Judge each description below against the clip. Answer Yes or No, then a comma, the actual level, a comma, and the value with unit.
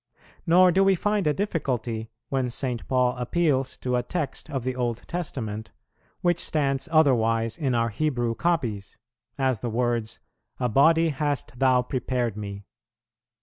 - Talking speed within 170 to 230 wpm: No, average, 145 wpm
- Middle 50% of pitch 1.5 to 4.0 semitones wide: No, average, 4.7 semitones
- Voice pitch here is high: No, low, 130 Hz